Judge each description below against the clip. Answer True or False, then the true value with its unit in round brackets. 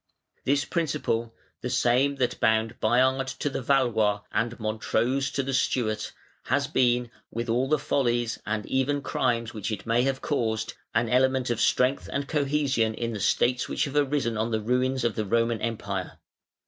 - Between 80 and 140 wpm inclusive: False (175 wpm)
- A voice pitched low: True (120 Hz)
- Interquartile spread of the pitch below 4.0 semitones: True (2.8 semitones)